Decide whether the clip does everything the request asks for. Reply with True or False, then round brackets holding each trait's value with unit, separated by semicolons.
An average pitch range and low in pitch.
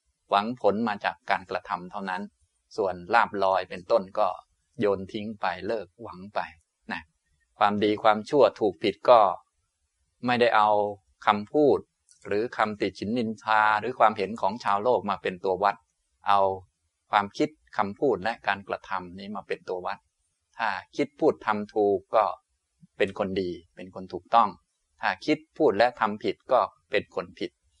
True (3.1 semitones; 100 Hz)